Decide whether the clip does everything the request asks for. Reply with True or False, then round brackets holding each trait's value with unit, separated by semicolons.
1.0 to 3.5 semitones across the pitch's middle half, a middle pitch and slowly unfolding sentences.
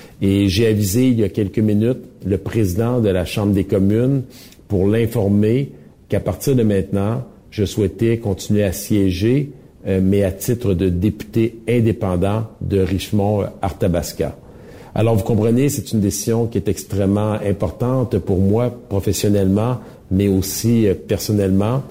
False (2.7 semitones; 105 Hz; 140 wpm)